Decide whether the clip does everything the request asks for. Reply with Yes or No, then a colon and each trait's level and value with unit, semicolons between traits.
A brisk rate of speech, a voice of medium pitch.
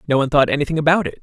Yes: fast, 295 wpm; medium, 150 Hz